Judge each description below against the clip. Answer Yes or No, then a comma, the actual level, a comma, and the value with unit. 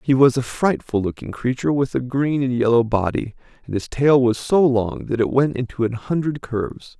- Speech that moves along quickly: Yes, fast, 215 wpm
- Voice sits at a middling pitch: No, low, 125 Hz